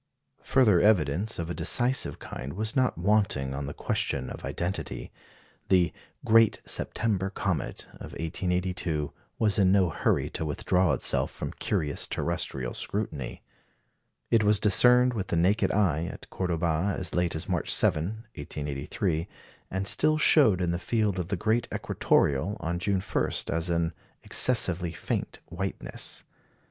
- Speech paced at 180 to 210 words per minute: No, average, 145 wpm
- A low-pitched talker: Yes, very low, 90 Hz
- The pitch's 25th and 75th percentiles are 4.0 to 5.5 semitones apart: Yes, average, 4.4 semitones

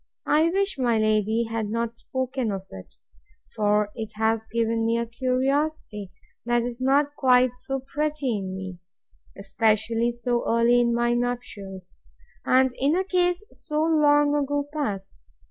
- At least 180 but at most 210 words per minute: No, average, 145 wpm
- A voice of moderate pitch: No, high, 240 Hz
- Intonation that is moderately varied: Yes, average, 4.1 semitones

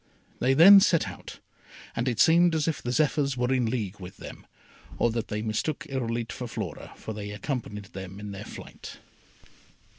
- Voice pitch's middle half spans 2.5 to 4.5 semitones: No, average, 5.0 semitones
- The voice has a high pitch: No, low, 120 Hz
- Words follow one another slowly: No, average, 180 wpm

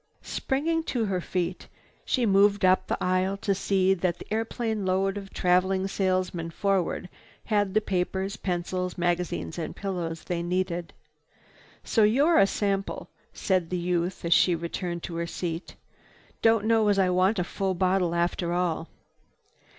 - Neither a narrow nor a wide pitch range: No, narrow, 2.1 semitones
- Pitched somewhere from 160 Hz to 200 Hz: Yes, medium, 185 Hz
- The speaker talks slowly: No, average, 155 wpm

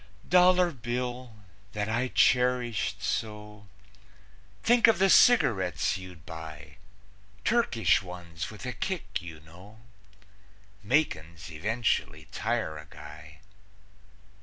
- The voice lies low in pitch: Yes, low, 105 Hz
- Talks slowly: Yes, slow, 100 wpm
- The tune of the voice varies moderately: No, wide, 7.2 semitones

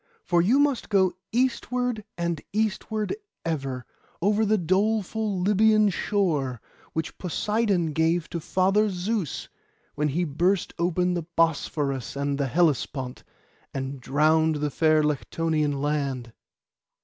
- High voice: No, medium, 170 Hz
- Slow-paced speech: Yes, slow, 120 wpm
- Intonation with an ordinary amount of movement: No, wide, 5.7 semitones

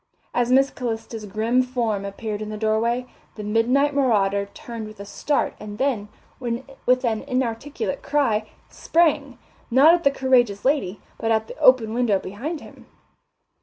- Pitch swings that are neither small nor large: Yes, average, 3.7 semitones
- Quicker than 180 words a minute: No, average, 155 wpm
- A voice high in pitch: Yes, high, 235 Hz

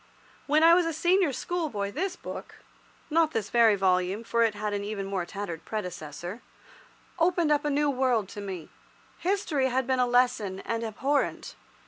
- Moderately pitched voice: No, high, 235 Hz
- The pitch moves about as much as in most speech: No, wide, 6.8 semitones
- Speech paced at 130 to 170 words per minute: Yes, average, 160 wpm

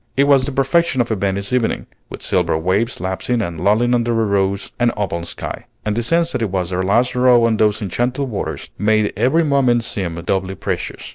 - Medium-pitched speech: No, low, 110 Hz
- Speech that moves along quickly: Yes, fast, 210 wpm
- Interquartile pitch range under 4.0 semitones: No, average, 4.4 semitones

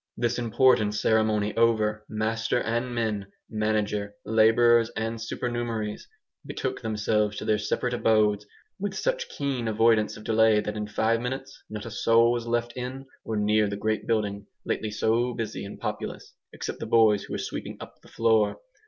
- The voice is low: Yes, low, 110 Hz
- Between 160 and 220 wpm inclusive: Yes, average, 165 wpm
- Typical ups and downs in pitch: No, narrow, 1.8 semitones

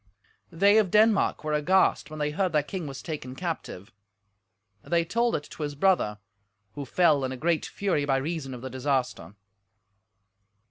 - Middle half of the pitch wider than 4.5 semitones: Yes, average, 5.1 semitones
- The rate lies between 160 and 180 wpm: Yes, average, 170 wpm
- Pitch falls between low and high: Yes, medium, 150 Hz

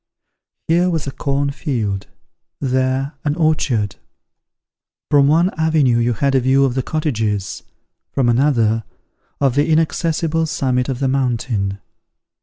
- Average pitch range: Yes, average, 4.2 semitones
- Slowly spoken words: Yes, slow, 130 wpm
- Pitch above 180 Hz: No, low, 135 Hz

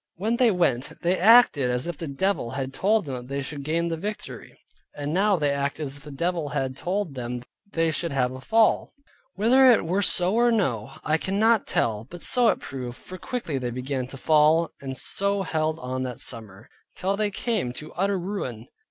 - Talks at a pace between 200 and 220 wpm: Yes, fast, 205 wpm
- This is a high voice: No, medium, 160 Hz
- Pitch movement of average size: No, wide, 7.0 semitones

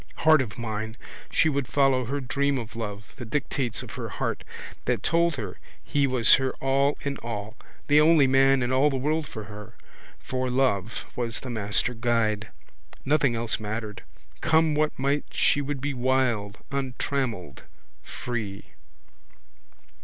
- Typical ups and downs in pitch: Yes, average, 3.7 semitones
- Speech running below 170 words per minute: Yes, average, 155 wpm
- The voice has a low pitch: Yes, low, 130 Hz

